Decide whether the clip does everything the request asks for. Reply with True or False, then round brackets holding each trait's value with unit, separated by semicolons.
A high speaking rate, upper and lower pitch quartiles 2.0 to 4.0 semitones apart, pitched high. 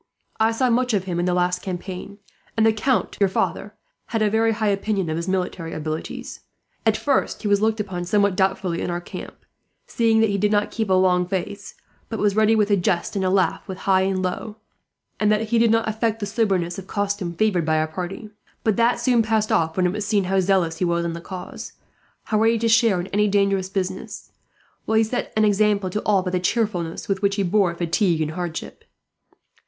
True (225 wpm; 3.2 semitones; 200 Hz)